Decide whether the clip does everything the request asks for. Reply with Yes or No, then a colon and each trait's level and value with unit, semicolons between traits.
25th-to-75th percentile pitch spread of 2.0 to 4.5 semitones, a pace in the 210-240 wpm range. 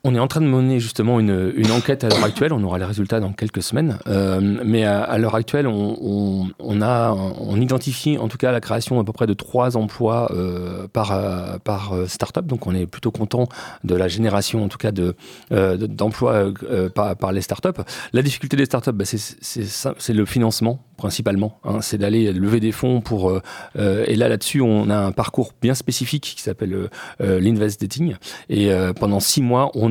Yes: average, 3.8 semitones; average, 215 wpm